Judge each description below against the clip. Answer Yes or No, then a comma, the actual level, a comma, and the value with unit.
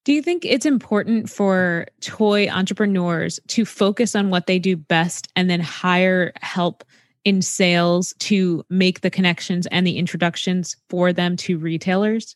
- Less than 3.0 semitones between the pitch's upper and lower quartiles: Yes, narrow, 2.6 semitones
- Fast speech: No, average, 155 wpm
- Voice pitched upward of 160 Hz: Yes, medium, 185 Hz